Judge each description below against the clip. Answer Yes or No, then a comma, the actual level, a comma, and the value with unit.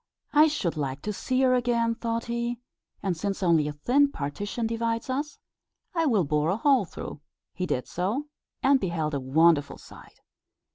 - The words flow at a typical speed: Yes, average, 175 wpm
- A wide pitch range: Yes, wide, 7.8 semitones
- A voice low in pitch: No, high, 215 Hz